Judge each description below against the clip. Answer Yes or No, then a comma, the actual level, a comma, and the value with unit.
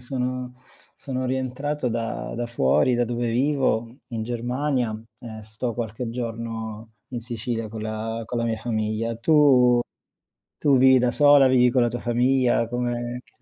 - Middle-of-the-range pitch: No, low, 120 Hz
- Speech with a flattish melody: Yes, narrow, 1.9 semitones